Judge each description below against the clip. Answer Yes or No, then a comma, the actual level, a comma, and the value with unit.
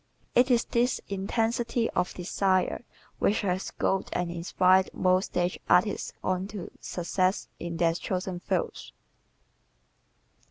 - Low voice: No, medium, 185 Hz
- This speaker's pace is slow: Yes, slow, 120 wpm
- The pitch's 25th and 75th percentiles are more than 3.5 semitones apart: No, average, 3.1 semitones